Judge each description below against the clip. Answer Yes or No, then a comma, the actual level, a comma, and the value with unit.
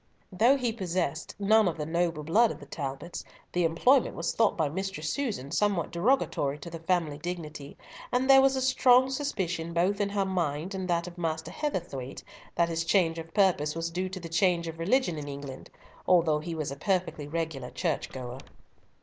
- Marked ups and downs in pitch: No, average, 4.0 semitones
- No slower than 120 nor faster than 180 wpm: No, average, 190 wpm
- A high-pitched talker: No, medium, 170 Hz